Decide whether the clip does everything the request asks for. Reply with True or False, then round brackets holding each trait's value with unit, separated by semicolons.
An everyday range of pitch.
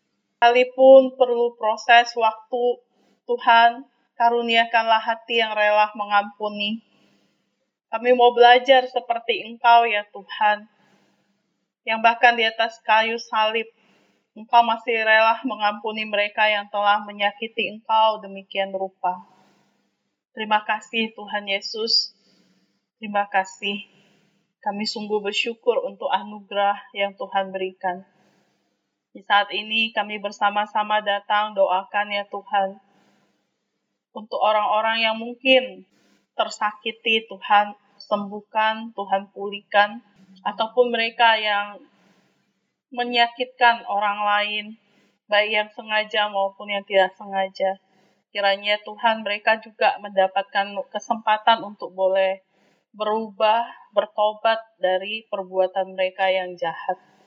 False (2.2 semitones)